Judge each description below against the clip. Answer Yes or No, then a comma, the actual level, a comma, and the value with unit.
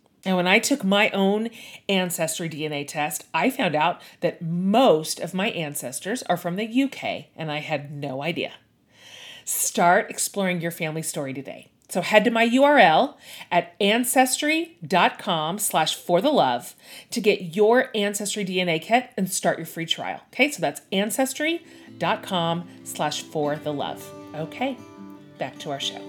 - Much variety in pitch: Yes, wide, 6.1 semitones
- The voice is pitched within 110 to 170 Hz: No, medium, 180 Hz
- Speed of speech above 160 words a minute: No, average, 145 wpm